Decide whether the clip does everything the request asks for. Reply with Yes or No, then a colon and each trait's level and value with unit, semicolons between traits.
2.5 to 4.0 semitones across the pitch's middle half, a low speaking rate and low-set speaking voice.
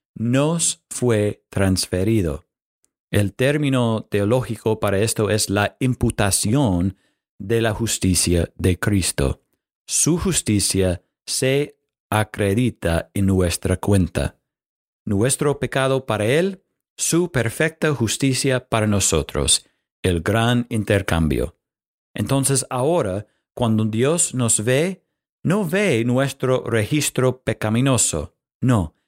No: average, 4.9 semitones; slow, 95 wpm; low, 115 Hz